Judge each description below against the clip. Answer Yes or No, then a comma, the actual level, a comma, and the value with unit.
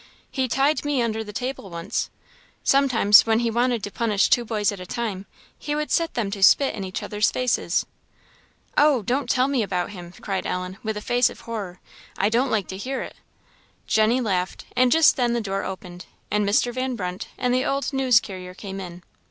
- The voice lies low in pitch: No, high, 220 Hz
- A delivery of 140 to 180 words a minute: No, fast, 205 wpm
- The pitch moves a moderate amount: Yes, average, 4.5 semitones